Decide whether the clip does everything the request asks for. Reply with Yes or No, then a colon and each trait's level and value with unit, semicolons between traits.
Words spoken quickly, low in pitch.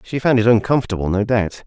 Yes: fast, 215 wpm; low, 110 Hz